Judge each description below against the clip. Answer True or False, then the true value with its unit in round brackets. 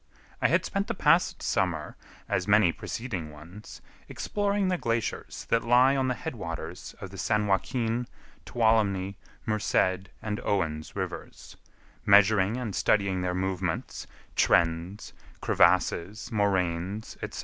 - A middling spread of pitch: True (4.0 semitones)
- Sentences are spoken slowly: True (125 wpm)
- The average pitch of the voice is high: False (100 Hz)